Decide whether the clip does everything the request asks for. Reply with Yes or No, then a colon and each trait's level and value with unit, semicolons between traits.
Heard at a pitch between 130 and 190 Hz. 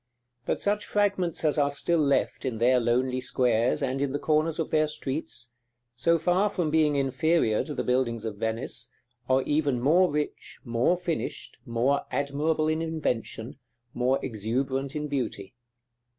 Yes: medium, 140 Hz